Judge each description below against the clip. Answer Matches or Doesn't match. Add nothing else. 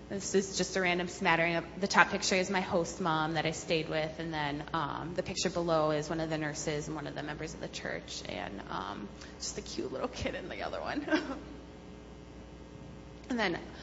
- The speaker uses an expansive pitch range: Doesn't match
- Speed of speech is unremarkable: Doesn't match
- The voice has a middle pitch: Matches